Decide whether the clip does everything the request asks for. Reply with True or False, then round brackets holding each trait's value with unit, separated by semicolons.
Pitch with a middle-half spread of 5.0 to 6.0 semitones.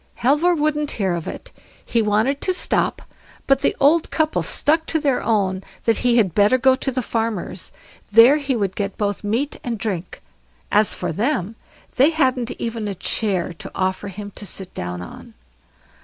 True (5.4 semitones)